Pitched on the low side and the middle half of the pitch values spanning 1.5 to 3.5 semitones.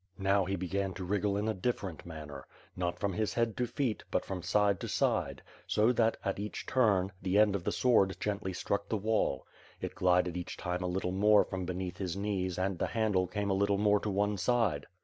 Yes: low, 100 Hz; narrow, 2.4 semitones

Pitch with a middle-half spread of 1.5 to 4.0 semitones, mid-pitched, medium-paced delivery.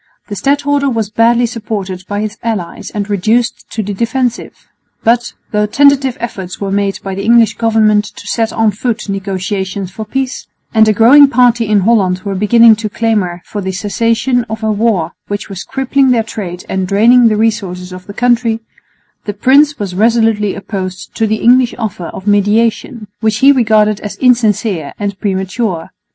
No: average, 2.9 semitones; high, 215 Hz; average, 175 wpm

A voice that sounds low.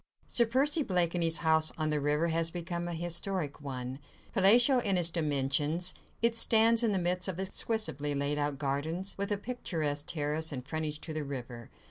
No: medium, 165 Hz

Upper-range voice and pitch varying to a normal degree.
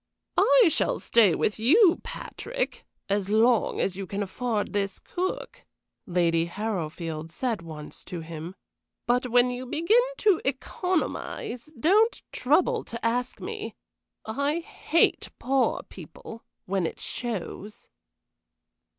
No: high, 235 Hz; wide, 8.2 semitones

